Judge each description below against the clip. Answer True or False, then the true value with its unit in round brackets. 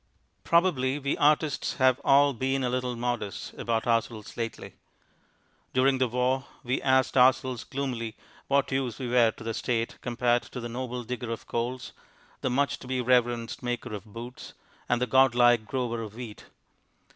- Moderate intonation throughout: False (1.9 semitones)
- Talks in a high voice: False (125 Hz)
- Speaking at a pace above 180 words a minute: False (170 wpm)